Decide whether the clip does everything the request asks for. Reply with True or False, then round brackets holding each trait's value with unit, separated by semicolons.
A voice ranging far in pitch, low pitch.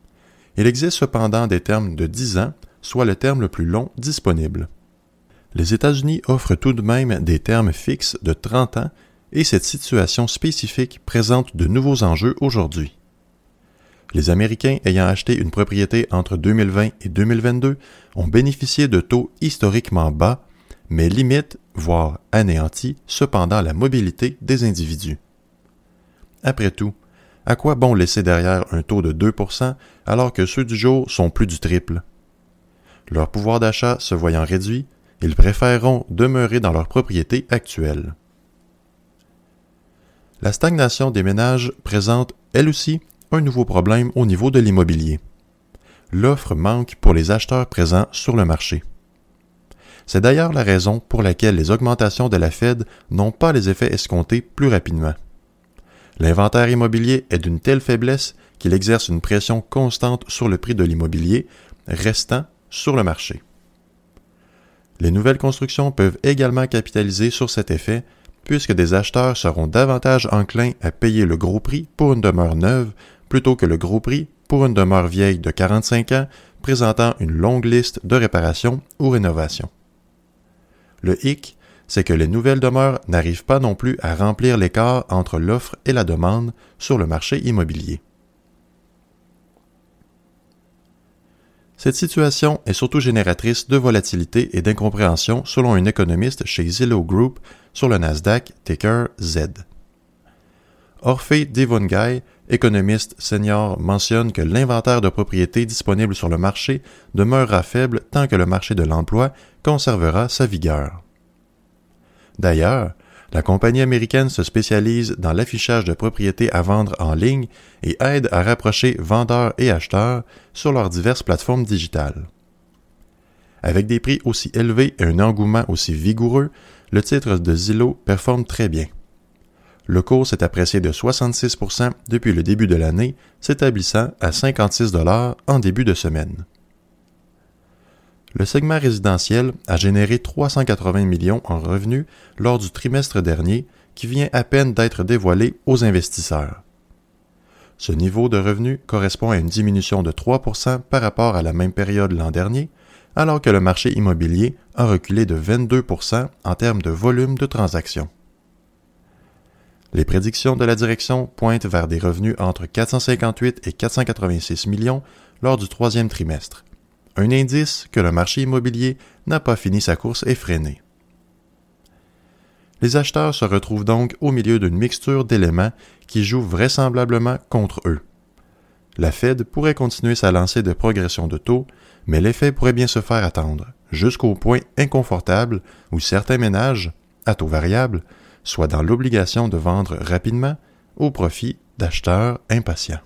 True (5.8 semitones; 110 Hz)